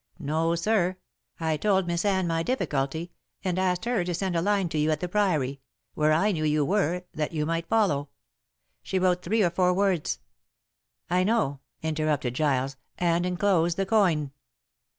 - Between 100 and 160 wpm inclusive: No, average, 175 wpm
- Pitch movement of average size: Yes, average, 3.6 semitones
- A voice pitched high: No, medium, 170 Hz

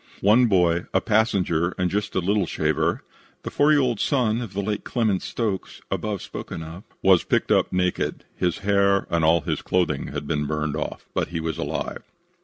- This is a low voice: Yes, very low, 95 Hz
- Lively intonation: No, average, 4.1 semitones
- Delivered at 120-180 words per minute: No, average, 195 wpm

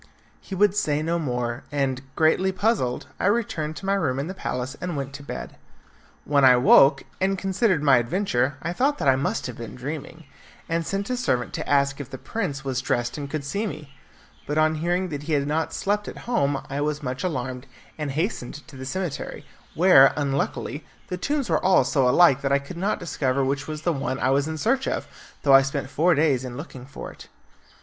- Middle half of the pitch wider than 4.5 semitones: Yes, average, 4.9 semitones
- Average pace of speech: No, fast, 215 wpm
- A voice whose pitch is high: No, medium, 145 Hz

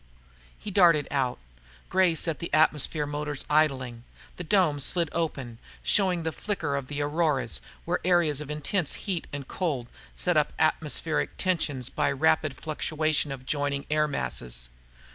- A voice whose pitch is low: No, medium, 150 Hz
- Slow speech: No, average, 145 wpm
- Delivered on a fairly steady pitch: No, average, 3.4 semitones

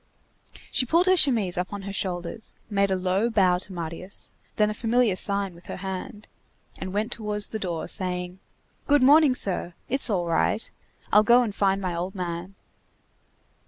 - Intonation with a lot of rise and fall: No, average, 3.4 semitones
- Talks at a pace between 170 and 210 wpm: Yes, average, 175 wpm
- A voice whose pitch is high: Yes, high, 195 Hz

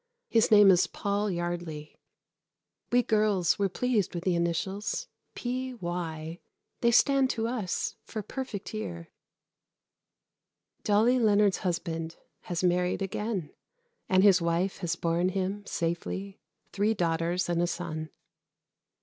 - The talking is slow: Yes, slow, 120 wpm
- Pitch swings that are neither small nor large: Yes, average, 3.6 semitones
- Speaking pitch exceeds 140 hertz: Yes, medium, 185 Hz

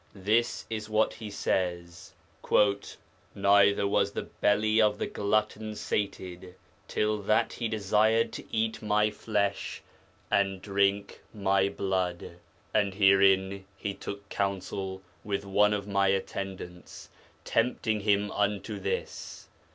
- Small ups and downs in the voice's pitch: Yes, narrow, 1.7 semitones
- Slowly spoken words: Yes, slow, 120 wpm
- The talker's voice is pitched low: Yes, low, 100 Hz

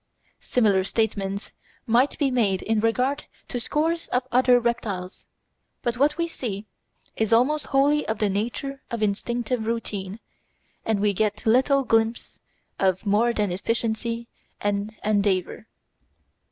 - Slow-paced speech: Yes, slow, 130 wpm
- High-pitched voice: Yes, high, 225 Hz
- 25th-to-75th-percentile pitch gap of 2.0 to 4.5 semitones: Yes, average, 3.4 semitones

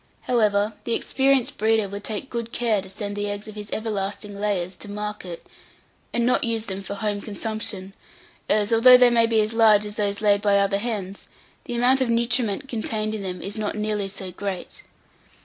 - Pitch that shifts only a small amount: Yes, narrow, 2.1 semitones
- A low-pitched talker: No, high, 210 Hz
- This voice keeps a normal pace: Yes, average, 195 wpm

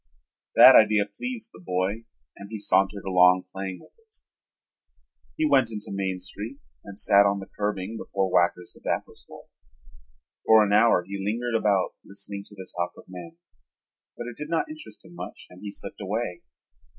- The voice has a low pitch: Yes, low, 100 Hz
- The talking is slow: No, average, 175 wpm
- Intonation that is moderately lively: Yes, average, 3.2 semitones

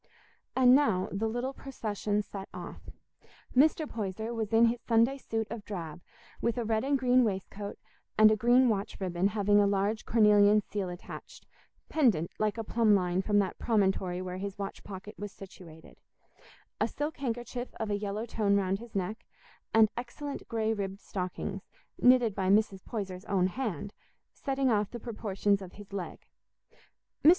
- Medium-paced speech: Yes, average, 165 wpm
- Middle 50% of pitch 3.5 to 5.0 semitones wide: No, average, 3.1 semitones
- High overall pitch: Yes, high, 210 Hz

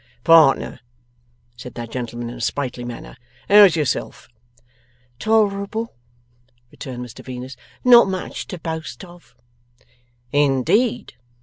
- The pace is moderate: No, slow, 110 wpm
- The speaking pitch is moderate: Yes, medium, 150 Hz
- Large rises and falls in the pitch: Yes, wide, 8.2 semitones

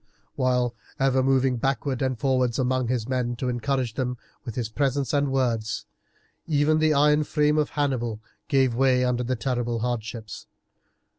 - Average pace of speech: Yes, average, 155 wpm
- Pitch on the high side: No, low, 130 Hz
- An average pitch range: No, narrow, 2.1 semitones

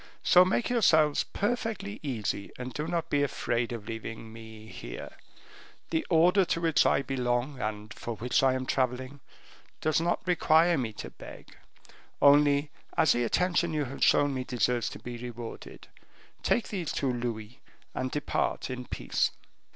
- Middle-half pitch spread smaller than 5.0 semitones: No, average, 5.3 semitones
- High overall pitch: No, low, 135 Hz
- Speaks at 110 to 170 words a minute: Yes, average, 160 wpm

